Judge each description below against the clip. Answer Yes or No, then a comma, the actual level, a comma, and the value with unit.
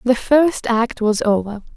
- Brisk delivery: No, average, 170 wpm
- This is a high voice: Yes, high, 235 Hz